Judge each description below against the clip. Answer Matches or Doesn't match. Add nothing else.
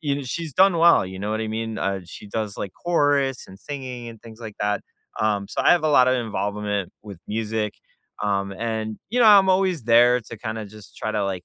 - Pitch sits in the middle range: Doesn't match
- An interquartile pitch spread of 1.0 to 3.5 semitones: Doesn't match